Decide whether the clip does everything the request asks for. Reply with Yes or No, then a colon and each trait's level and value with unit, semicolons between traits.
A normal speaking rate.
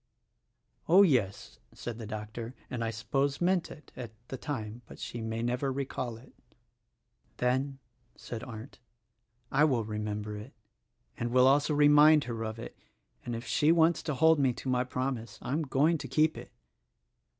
Yes: average, 185 wpm